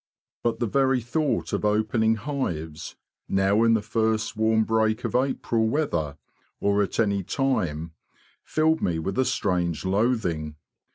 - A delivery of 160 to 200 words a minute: No, average, 145 wpm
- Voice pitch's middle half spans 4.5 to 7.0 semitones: No, average, 4.0 semitones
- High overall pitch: No, low, 110 Hz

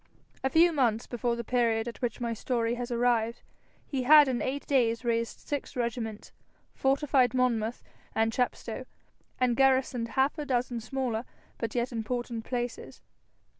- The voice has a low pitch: No, high, 245 Hz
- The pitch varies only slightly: Yes, narrow, 2.1 semitones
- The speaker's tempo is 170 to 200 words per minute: No, average, 150 wpm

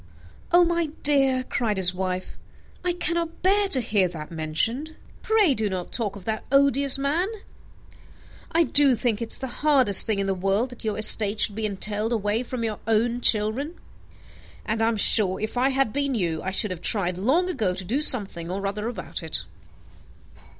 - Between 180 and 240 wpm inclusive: Yes, average, 190 wpm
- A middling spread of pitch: No, wide, 5.7 semitones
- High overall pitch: Yes, high, 225 Hz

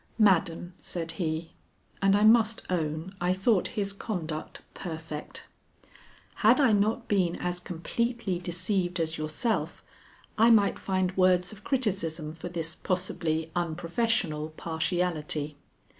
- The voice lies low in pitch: No, medium, 180 Hz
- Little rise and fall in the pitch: No, average, 3.9 semitones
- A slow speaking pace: Yes, slow, 120 wpm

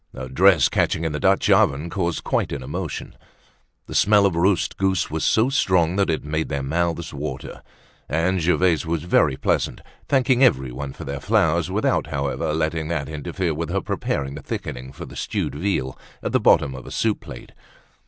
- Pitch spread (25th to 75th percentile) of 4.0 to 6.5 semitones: Yes, average, 4.7 semitones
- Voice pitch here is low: Yes, very low, 80 Hz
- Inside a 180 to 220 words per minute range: Yes, average, 185 wpm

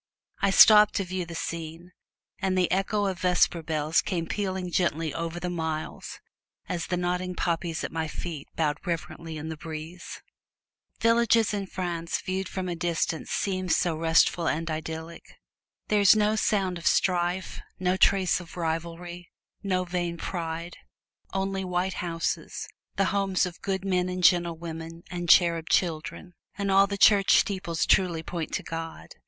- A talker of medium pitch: Yes, medium, 175 Hz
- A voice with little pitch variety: Yes, narrow, 2.3 semitones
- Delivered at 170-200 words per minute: No, average, 160 wpm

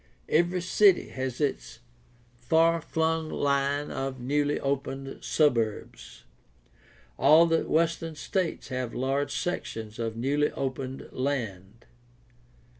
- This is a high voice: No, medium, 140 Hz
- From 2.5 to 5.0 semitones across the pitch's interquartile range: Yes, average, 3.9 semitones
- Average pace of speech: No, slow, 105 wpm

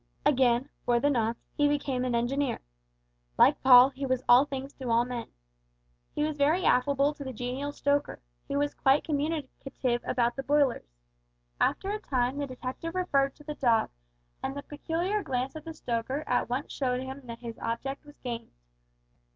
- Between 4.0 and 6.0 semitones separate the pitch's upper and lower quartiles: No, average, 2.8 semitones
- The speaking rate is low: No, average, 175 wpm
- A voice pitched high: Yes, very high, 270 Hz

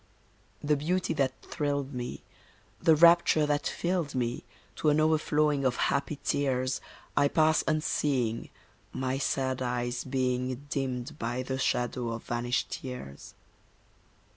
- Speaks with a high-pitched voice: No, low, 135 Hz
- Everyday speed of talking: No, slow, 125 wpm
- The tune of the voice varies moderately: Yes, average, 3.2 semitones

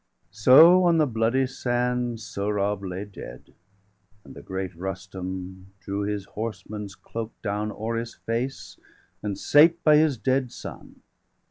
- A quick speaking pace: No, slow, 135 wpm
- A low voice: Yes, low, 110 Hz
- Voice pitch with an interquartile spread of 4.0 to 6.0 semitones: Yes, average, 4.4 semitones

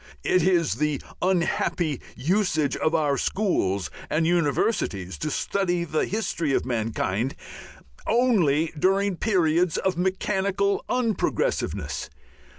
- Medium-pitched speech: Yes, medium, 170 Hz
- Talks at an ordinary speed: No, slow, 105 wpm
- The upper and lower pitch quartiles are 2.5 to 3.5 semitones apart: No, average, 5.0 semitones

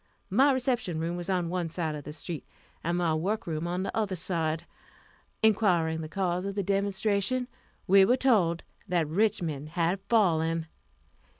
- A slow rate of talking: No, average, 170 wpm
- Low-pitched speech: No, medium, 180 Hz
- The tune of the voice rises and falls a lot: No, average, 3.5 semitones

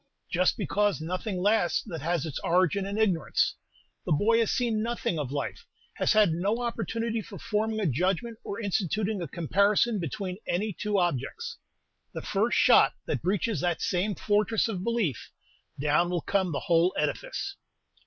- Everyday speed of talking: Yes, average, 165 wpm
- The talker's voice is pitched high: Yes, high, 195 Hz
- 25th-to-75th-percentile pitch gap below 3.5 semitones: No, average, 3.9 semitones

